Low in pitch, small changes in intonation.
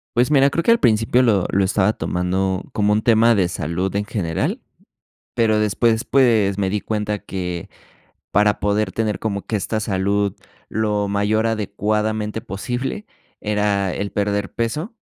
Yes: low, 105 Hz; narrow, 2.1 semitones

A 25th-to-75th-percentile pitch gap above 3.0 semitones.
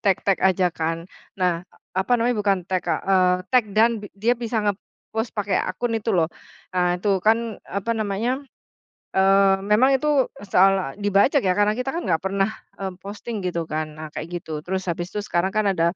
Yes: average, 3.4 semitones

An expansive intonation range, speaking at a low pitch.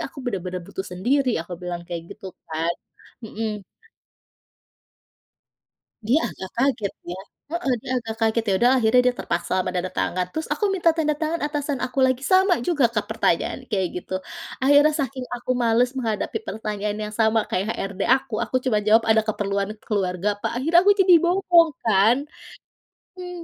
No: wide, 5.8 semitones; high, 230 Hz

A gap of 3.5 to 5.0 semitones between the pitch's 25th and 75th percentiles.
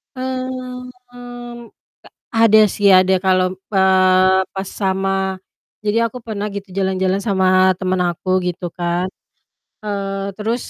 No: average, 3.1 semitones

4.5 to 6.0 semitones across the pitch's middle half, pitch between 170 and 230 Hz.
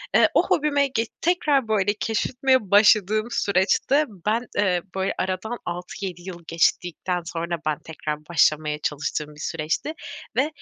Yes: wide, 5.5 semitones; high, 190 Hz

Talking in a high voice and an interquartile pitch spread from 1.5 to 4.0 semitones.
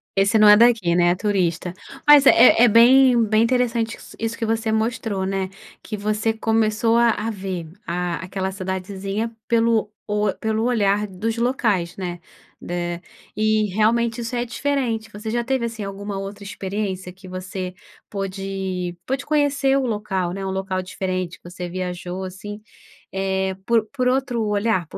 Yes: high, 210 Hz; average, 3.4 semitones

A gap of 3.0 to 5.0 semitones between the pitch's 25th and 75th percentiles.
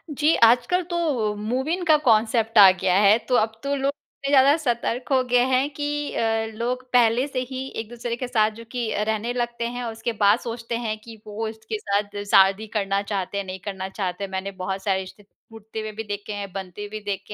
Yes: average, 3.3 semitones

